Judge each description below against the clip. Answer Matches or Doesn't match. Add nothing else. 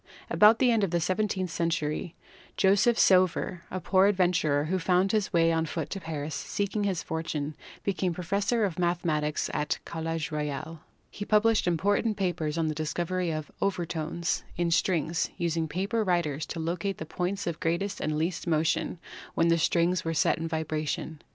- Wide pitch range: Doesn't match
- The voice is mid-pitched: Matches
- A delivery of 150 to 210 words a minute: Matches